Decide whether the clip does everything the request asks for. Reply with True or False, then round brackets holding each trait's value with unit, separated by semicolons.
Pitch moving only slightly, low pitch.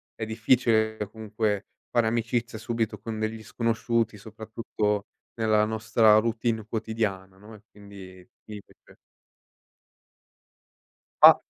True (1.3 semitones; 110 Hz)